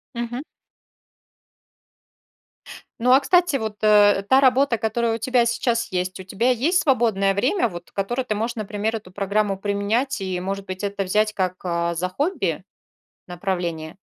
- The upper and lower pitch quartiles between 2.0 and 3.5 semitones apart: No, average, 4.0 semitones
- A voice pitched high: Yes, high, 210 Hz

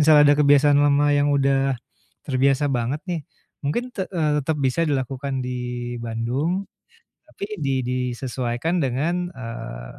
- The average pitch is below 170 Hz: Yes, medium, 140 Hz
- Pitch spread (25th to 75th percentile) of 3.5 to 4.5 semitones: No, average, 2.8 semitones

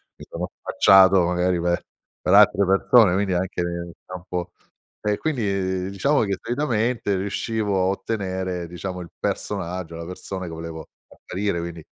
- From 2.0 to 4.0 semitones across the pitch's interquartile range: Yes, narrow, 2.6 semitones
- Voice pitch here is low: Yes, very low, 95 Hz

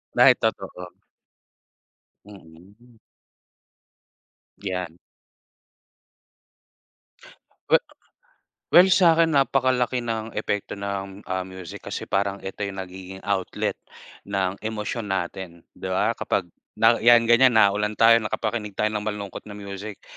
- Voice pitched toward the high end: No, low, 100 Hz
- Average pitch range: Yes, average, 3.0 semitones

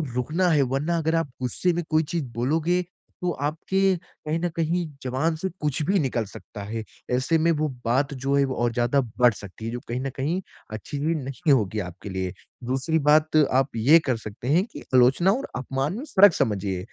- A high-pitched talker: No, medium, 140 Hz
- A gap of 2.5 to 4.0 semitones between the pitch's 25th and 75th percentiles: No, average, 5.2 semitones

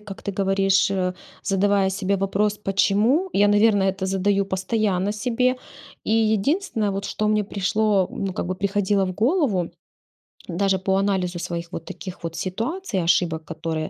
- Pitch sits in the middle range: No, high, 195 Hz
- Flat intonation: Yes, narrow, 2.2 semitones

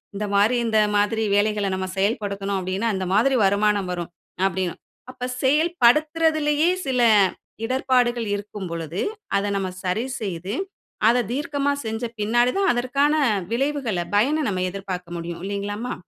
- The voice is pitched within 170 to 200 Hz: No, high, 215 Hz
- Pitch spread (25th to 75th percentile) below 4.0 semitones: No, average, 4.9 semitones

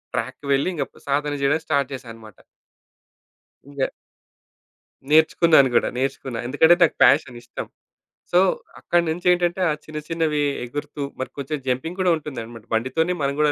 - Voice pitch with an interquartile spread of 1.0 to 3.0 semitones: No, average, 3.7 semitones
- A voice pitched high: No, medium, 145 Hz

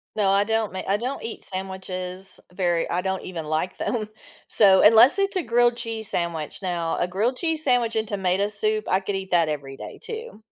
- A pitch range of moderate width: Yes, average, 3.8 semitones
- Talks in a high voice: Yes, high, 195 Hz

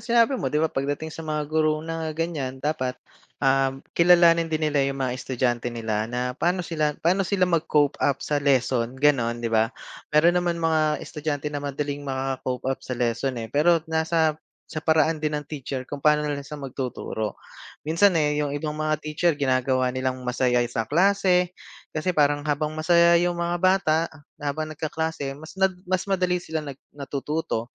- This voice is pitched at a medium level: Yes, medium, 150 Hz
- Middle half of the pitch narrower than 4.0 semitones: Yes, average, 3.5 semitones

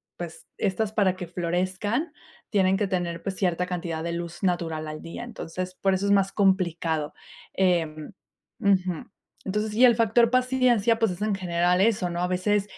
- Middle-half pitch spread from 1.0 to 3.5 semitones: Yes, average, 3.2 semitones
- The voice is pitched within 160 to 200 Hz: Yes, medium, 185 Hz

